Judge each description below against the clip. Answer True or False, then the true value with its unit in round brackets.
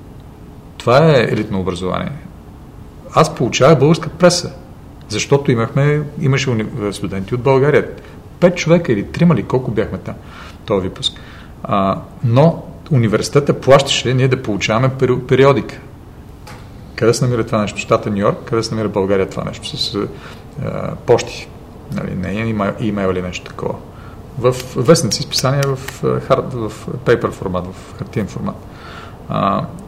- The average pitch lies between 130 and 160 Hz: False (120 Hz)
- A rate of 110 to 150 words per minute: True (135 wpm)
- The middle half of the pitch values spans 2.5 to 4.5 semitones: False (5.3 semitones)